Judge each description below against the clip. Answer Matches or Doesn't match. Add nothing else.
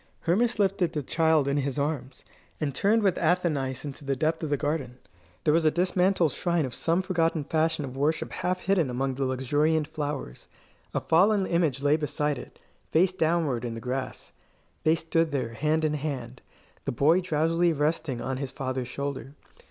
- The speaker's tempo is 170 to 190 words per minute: Matches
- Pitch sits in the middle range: Matches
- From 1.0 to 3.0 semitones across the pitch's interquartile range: Doesn't match